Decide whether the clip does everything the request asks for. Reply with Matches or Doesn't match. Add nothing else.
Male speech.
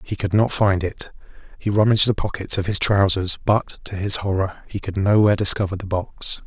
Matches